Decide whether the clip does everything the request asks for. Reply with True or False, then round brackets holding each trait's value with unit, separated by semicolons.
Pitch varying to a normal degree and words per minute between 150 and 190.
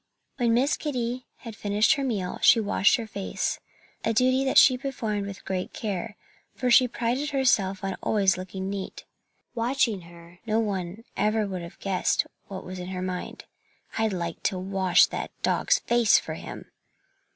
True (4.2 semitones; 170 wpm)